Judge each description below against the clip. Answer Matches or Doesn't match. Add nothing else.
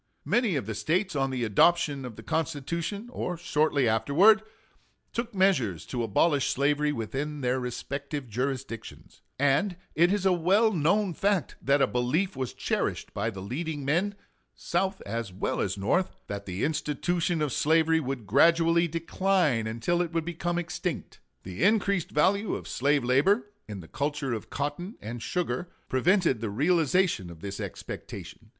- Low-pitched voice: Doesn't match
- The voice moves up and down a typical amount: Doesn't match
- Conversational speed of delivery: Matches